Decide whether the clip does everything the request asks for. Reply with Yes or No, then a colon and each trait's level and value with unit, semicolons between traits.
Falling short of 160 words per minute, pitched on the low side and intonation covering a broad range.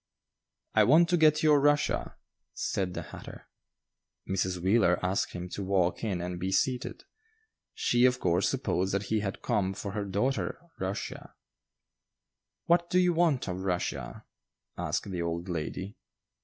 Yes: average, 150 wpm; low, 100 Hz; wide, 6.6 semitones